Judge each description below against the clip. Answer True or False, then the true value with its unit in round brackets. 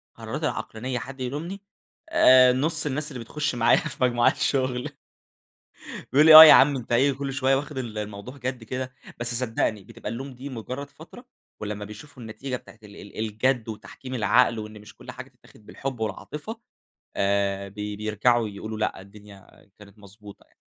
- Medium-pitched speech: False (125 Hz)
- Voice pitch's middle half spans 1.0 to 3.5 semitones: False (4.1 semitones)